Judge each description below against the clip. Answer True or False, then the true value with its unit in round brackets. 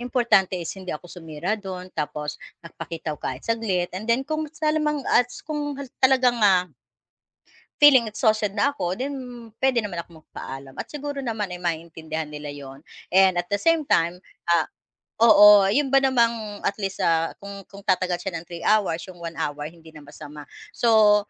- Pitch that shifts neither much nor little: False (6.1 semitones)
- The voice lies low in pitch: False (195 Hz)